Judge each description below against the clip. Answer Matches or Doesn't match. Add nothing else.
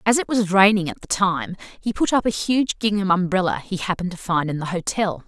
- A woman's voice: Matches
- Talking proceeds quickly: Matches